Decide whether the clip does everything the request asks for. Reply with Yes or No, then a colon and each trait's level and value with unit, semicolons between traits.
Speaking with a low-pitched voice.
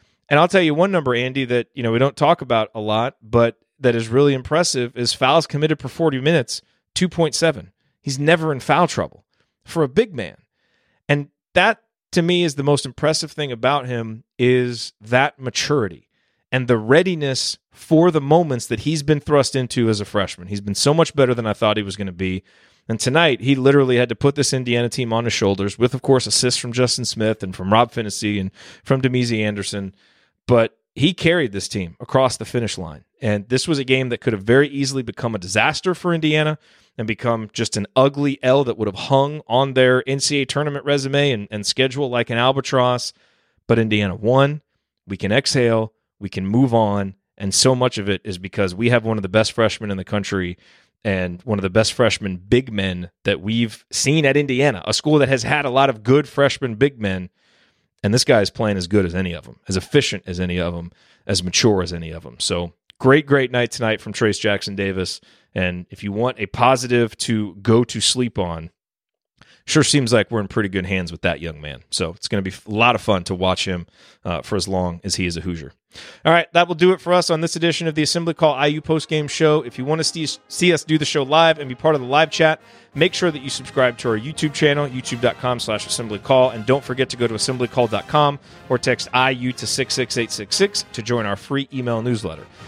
Yes: low, 125 Hz